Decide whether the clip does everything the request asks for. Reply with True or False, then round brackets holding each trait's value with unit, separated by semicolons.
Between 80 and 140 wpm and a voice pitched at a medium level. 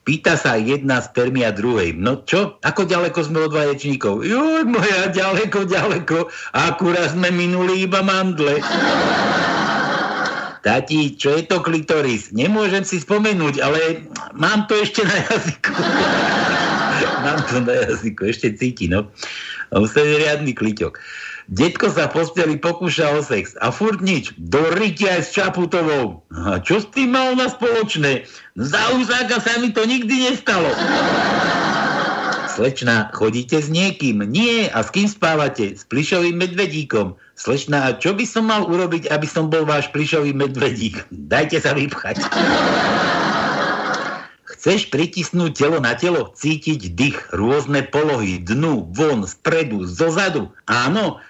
True (135 wpm; 165 Hz)